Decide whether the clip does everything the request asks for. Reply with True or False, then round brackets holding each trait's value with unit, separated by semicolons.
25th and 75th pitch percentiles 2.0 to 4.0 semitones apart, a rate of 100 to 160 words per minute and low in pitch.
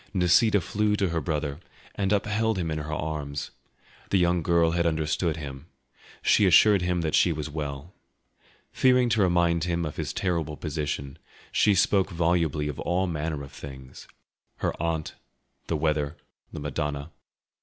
True (3.1 semitones; 155 wpm; 80 Hz)